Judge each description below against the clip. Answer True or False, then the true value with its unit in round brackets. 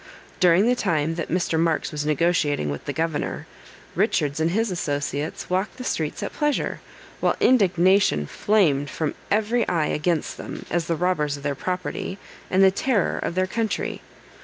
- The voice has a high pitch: False (170 Hz)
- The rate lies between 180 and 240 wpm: False (165 wpm)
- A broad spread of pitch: False (4.2 semitones)